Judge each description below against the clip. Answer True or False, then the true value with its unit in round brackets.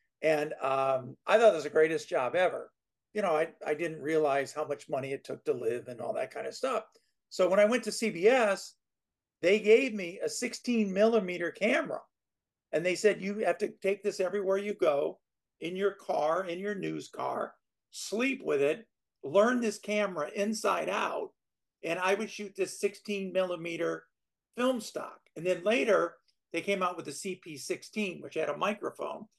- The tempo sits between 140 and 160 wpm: False (185 wpm)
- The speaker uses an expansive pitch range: False (4.1 semitones)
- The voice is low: False (195 Hz)